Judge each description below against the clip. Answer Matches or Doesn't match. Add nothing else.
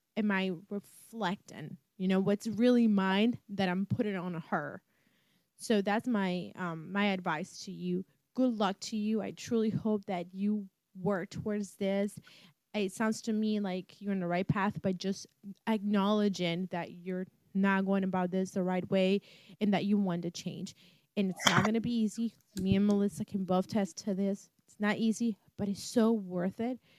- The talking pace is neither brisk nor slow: Matches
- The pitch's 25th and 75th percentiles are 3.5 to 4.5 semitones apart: Doesn't match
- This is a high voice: Matches